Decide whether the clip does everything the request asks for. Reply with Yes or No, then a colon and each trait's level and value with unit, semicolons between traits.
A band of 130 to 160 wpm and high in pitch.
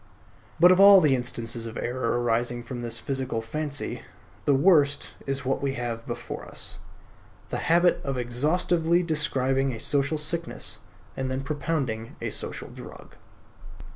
No: average, 145 wpm; low, 135 Hz